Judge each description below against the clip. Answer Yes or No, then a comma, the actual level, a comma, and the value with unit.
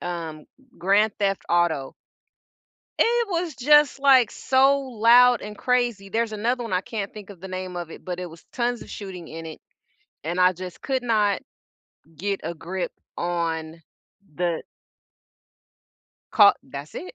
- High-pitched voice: Yes, high, 200 Hz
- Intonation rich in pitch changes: Yes, wide, 5.8 semitones